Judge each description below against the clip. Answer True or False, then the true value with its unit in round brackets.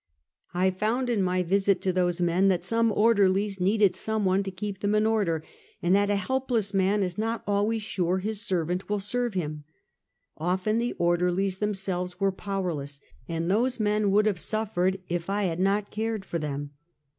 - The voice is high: True (195 Hz)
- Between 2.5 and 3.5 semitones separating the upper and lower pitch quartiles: True (2.8 semitones)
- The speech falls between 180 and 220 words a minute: True (185 wpm)